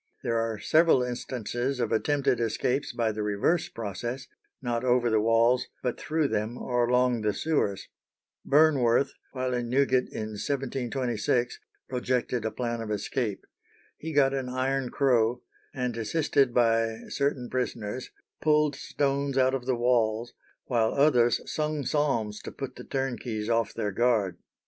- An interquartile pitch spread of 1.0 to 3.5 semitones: Yes, average, 2.9 semitones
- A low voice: Yes, low, 125 Hz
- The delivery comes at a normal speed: Yes, average, 145 wpm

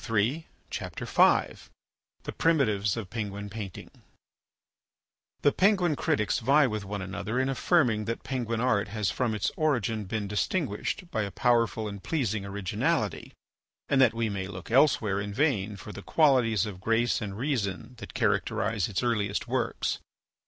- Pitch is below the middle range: Yes, low, 110 Hz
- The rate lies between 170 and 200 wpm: No, average, 150 wpm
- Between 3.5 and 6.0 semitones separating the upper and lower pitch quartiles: Yes, average, 4.0 semitones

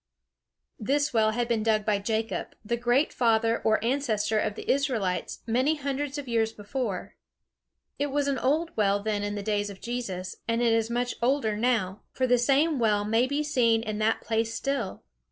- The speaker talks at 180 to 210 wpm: Yes, average, 190 wpm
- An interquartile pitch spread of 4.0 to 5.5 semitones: No, average, 3.6 semitones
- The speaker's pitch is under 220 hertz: No, high, 230 Hz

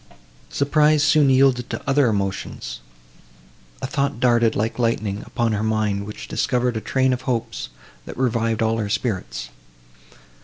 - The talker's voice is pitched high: No, low, 115 Hz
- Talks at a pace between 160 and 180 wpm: No, average, 145 wpm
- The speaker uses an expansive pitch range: No, average, 3.6 semitones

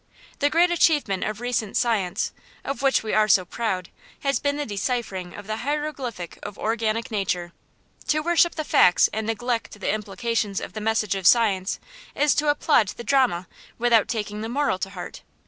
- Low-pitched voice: No, high, 225 Hz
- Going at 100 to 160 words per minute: No, average, 180 wpm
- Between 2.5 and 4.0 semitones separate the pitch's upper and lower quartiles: No, average, 5.3 semitones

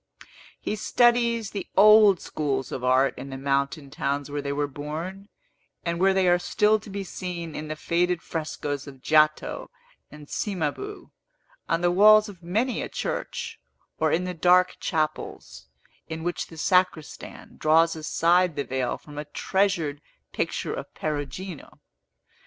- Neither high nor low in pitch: Yes, medium, 165 Hz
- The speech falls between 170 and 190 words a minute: No, average, 150 wpm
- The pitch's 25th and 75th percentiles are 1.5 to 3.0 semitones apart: No, average, 4.6 semitones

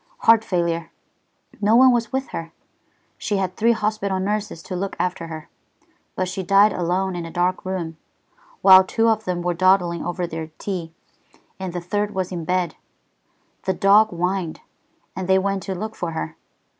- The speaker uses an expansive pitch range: No, average, 2.7 semitones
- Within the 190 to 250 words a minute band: No, average, 175 wpm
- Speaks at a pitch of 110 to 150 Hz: No, medium, 185 Hz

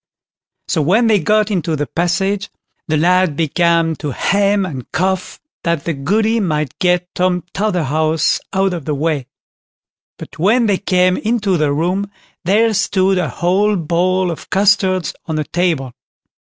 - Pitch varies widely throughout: No, average, 3.8 semitones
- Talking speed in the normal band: Yes, average, 150 wpm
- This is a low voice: No, medium, 180 Hz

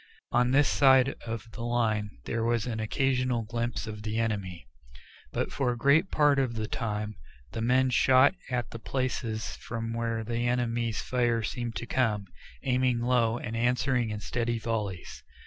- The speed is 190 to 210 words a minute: No, average, 165 wpm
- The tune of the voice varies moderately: No, narrow, 2.0 semitones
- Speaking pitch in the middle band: No, low, 120 Hz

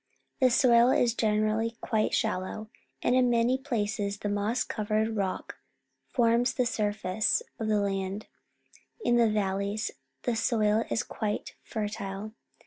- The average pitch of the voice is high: Yes, high, 215 Hz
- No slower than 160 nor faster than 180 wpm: No, slow, 135 wpm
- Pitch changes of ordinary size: No, narrow, 2.3 semitones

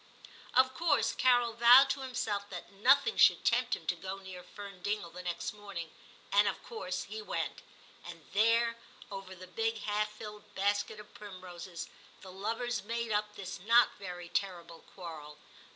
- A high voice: Yes, high, 205 Hz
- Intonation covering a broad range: No, average, 3.8 semitones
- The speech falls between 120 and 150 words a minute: No, average, 165 wpm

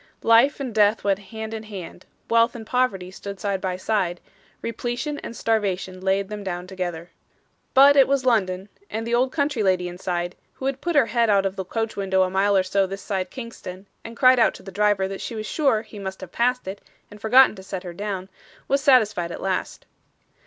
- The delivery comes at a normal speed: No, fast, 215 wpm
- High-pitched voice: Yes, high, 205 Hz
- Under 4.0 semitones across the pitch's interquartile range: Yes, average, 3.6 semitones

